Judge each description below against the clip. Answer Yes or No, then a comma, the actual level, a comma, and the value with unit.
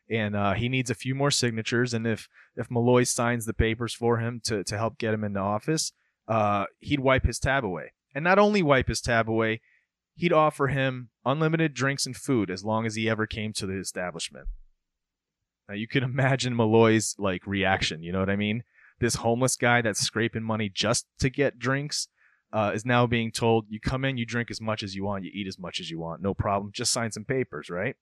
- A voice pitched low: Yes, low, 115 Hz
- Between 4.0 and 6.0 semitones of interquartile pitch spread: No, average, 3.3 semitones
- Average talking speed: No, fast, 225 wpm